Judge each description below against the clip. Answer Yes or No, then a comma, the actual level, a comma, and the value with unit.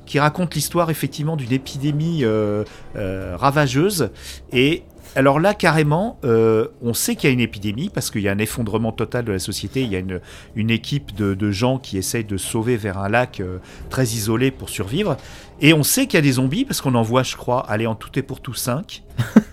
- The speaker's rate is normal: No, fast, 225 wpm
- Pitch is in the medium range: No, low, 125 Hz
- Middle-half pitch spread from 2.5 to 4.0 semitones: No, wide, 5.4 semitones